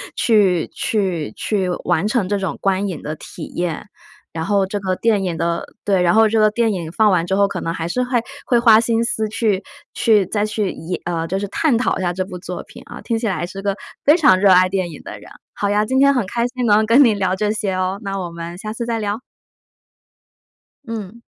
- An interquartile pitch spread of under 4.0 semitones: Yes, average, 3.4 semitones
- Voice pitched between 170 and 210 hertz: Yes, high, 200 Hz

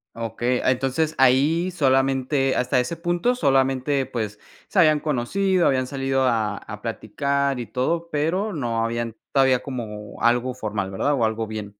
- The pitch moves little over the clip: No, average, 3.9 semitones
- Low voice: Yes, low, 130 Hz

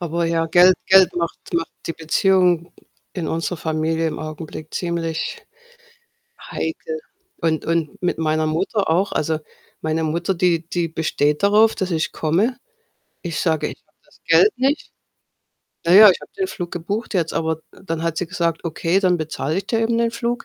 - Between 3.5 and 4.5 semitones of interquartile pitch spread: No, average, 2.9 semitones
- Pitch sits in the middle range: Yes, medium, 170 Hz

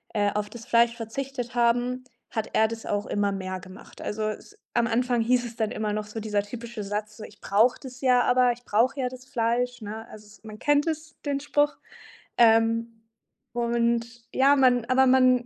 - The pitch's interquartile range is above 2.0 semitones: Yes, narrow, 2.6 semitones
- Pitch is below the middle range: No, high, 235 Hz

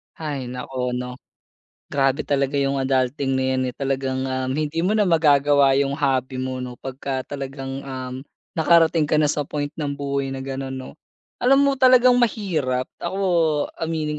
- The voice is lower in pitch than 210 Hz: Yes, medium, 140 Hz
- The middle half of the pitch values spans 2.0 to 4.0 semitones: Yes, average, 2.9 semitones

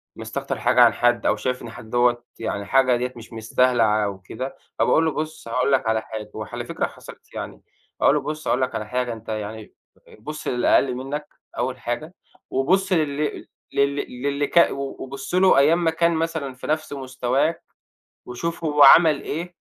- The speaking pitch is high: No, low, 135 Hz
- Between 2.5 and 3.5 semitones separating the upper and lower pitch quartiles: No, average, 4.2 semitones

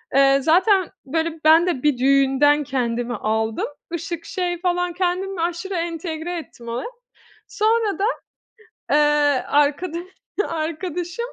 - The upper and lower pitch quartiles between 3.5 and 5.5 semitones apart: Yes, average, 4.4 semitones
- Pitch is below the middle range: No, very high, 325 Hz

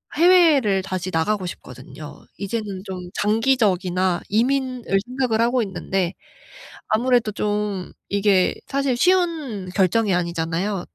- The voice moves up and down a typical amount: Yes, average, 5.0 semitones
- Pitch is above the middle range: Yes, high, 210 Hz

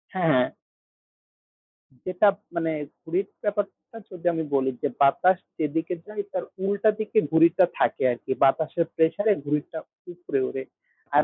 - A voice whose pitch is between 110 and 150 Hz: No, medium, 170 Hz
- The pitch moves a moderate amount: Yes, average, 4.2 semitones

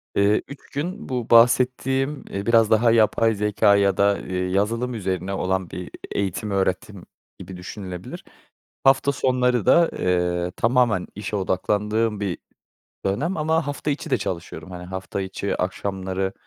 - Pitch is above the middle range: No, low, 105 Hz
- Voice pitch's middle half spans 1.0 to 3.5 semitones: No, average, 4.8 semitones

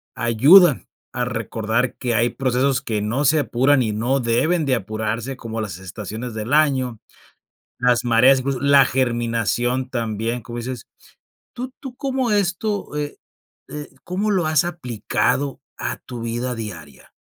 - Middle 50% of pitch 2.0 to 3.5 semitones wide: No, average, 3.9 semitones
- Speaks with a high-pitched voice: No, low, 125 Hz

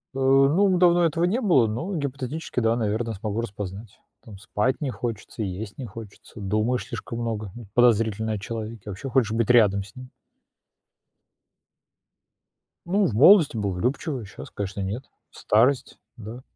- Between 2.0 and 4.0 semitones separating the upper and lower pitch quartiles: No, average, 4.5 semitones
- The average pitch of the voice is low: Yes, low, 115 Hz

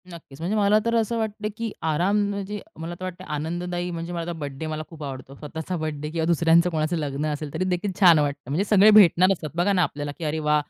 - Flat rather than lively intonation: No, average, 3.4 semitones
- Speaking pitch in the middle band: Yes, medium, 170 Hz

